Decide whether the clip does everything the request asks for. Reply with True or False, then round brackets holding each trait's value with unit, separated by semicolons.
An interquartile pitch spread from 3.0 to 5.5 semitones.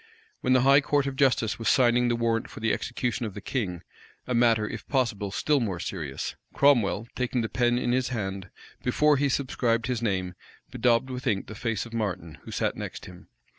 True (3.6 semitones)